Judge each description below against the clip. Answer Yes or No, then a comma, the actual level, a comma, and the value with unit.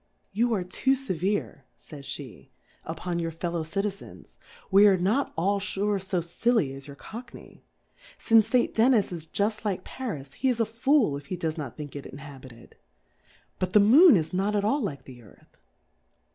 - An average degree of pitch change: No, wide, 6.2 semitones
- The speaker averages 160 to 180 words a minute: Yes, average, 165 wpm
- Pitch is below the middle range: No, medium, 185 Hz